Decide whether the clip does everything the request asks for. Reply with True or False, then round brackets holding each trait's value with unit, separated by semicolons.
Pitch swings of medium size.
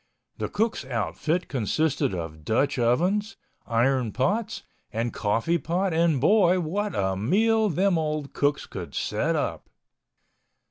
False (7.8 semitones)